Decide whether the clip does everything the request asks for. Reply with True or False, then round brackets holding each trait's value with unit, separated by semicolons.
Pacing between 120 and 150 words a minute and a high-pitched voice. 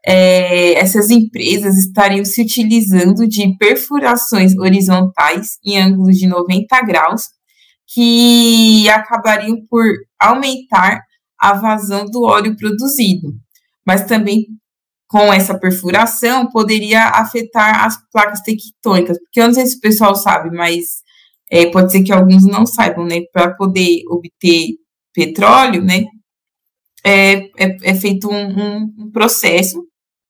True (125 wpm; 205 Hz)